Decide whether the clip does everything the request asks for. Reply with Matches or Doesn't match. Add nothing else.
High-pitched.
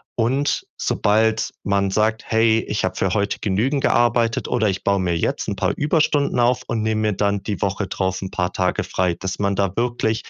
Doesn't match